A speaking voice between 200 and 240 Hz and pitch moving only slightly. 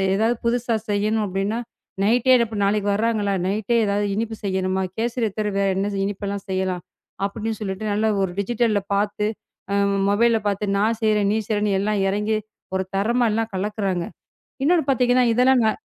Yes: high, 210 Hz; narrow, 2.2 semitones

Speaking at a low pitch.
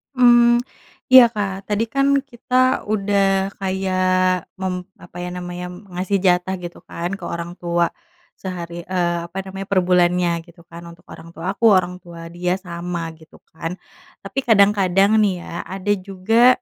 No: medium, 185 Hz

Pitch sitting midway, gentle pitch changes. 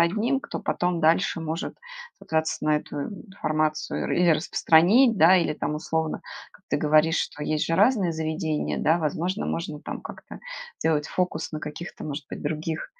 Yes: medium, 160 Hz; narrow, 2.3 semitones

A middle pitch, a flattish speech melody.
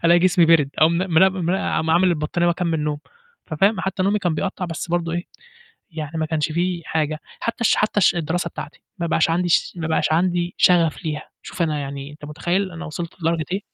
Yes: medium, 170 Hz; narrow, 2.3 semitones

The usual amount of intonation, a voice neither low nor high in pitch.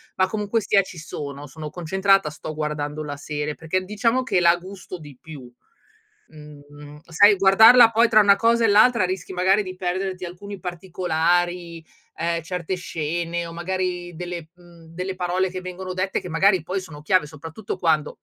Yes: average, 3.1 semitones; medium, 180 Hz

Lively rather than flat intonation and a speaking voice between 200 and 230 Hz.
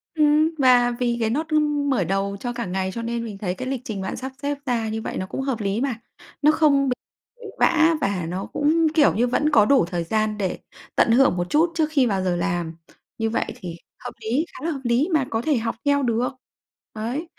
No: wide, 5.8 semitones; high, 240 Hz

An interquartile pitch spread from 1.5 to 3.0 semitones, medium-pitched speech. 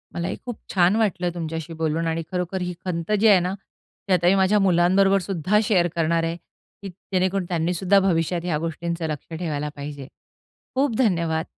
Yes: average, 2.7 semitones; medium, 175 Hz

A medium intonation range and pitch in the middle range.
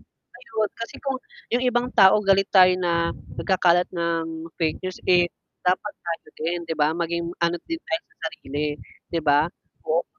Yes: average, 3.3 semitones; medium, 175 Hz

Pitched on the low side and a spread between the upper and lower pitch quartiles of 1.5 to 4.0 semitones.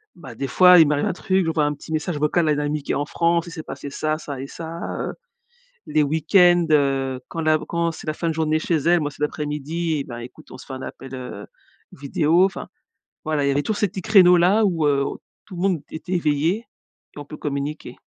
No: medium, 155 Hz; average, 2.9 semitones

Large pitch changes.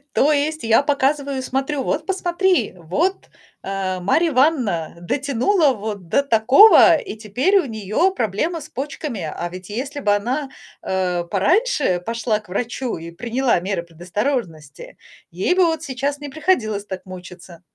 Yes: wide, 7.6 semitones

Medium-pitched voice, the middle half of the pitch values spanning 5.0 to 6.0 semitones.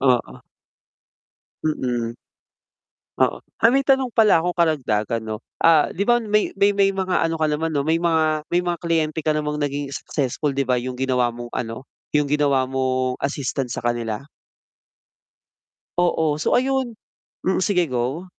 Yes: medium, 150 Hz; wide, 5.5 semitones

